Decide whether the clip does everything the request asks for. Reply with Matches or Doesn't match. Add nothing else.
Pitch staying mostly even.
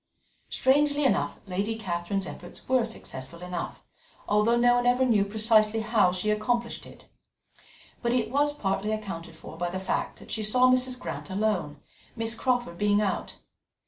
Doesn't match